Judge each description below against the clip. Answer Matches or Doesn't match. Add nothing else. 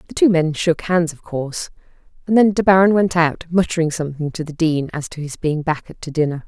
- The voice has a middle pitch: Matches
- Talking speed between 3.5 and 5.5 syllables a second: Doesn't match